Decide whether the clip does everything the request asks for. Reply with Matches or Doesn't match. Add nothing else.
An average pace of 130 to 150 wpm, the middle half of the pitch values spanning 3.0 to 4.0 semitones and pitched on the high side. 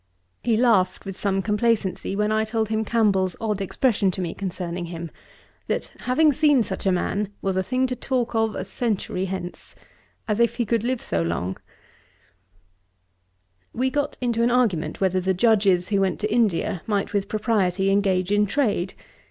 Doesn't match